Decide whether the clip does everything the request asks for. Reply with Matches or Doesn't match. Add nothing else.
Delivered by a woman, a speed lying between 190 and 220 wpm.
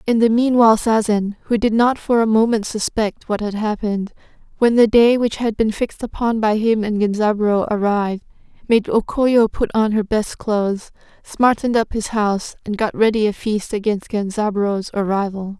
Doesn't match